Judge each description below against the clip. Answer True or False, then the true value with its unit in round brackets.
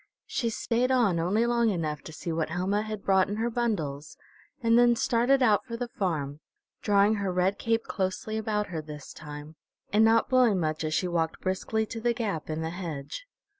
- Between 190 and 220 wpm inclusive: True (200 wpm)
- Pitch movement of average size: False (6.0 semitones)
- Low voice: False (200 Hz)